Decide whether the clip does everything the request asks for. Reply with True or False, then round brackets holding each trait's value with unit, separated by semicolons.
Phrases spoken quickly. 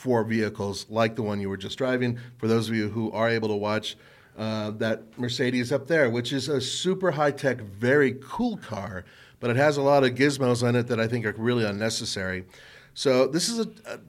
True (220 wpm)